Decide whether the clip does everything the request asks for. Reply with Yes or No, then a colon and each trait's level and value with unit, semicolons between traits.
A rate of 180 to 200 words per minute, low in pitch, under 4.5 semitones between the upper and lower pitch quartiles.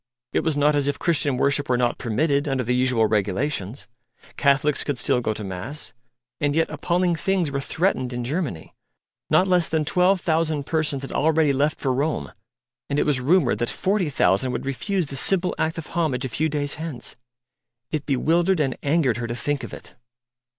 No: average, 190 wpm; medium, 145 Hz; average, 4.1 semitones